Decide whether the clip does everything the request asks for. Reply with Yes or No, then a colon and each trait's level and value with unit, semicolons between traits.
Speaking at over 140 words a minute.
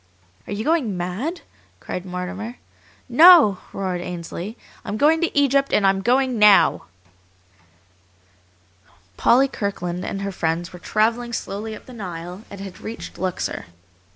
No: slow, 135 wpm